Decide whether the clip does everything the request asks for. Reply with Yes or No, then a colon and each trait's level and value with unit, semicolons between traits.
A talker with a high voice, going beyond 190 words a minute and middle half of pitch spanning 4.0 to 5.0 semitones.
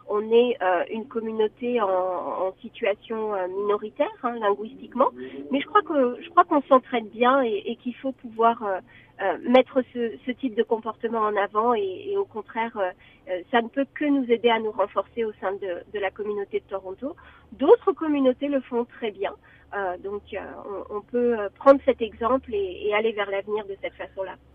Yes: high, 225 Hz; average, 200 wpm; average, 4.5 semitones